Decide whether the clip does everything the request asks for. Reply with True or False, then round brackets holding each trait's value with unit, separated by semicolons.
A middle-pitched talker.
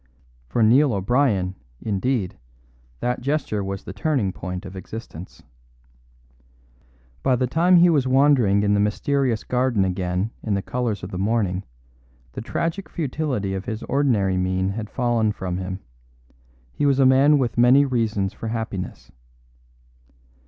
False (110 Hz)